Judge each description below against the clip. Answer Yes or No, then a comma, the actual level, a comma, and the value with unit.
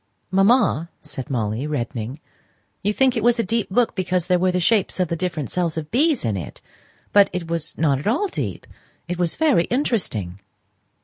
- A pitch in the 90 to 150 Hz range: No, medium, 180 Hz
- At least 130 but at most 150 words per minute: No, average, 190 wpm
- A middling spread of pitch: No, wide, 6.9 semitones